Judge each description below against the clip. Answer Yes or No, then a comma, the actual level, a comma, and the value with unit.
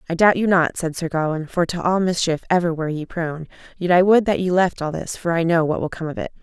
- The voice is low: No, medium, 170 Hz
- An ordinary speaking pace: No, fast, 290 wpm